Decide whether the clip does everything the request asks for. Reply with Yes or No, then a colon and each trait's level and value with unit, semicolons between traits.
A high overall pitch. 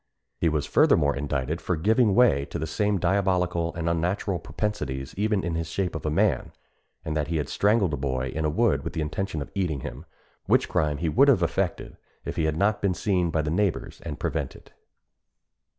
No: very low, 85 Hz